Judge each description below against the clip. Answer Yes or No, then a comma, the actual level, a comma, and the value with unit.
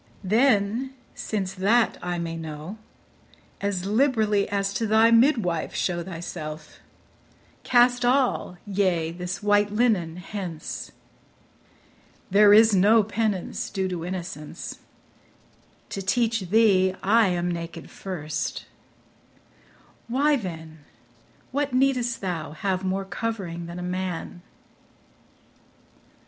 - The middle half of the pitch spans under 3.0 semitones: No, average, 4.2 semitones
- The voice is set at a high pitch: Yes, high, 195 Hz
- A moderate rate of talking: No, slow, 105 wpm